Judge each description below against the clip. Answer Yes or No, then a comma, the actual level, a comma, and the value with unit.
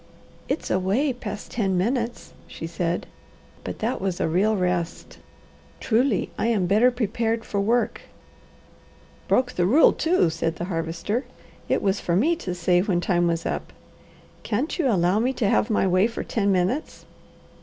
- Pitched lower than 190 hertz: No, high, 200 Hz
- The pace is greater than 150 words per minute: Yes, average, 165 wpm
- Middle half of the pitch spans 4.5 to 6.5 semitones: Yes, average, 4.9 semitones